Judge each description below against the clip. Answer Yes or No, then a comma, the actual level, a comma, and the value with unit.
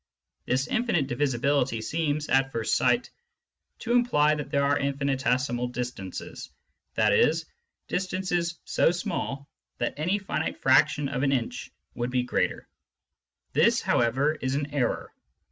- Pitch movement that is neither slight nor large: Yes, average, 3.6 semitones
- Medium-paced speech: No, slow, 130 wpm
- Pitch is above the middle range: No, medium, 140 Hz